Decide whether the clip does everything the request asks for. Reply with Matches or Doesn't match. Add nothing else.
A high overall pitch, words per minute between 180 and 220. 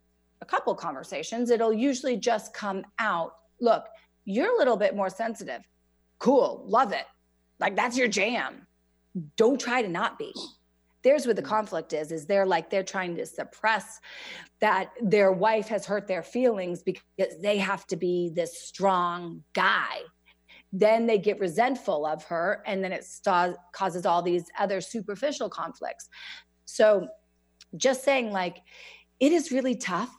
Doesn't match